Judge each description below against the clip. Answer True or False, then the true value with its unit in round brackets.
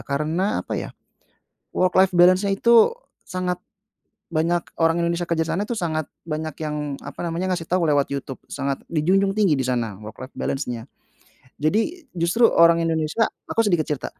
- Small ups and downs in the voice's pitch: False (3.6 semitones)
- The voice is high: False (170 Hz)